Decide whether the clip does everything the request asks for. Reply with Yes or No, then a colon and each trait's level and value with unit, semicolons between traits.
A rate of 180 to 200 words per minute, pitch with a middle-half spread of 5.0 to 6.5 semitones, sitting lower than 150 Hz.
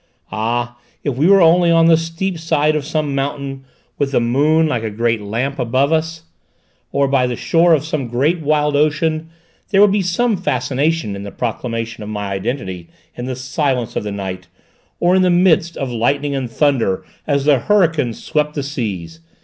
Yes: average, 185 wpm; average, 5.3 semitones; medium, 140 Hz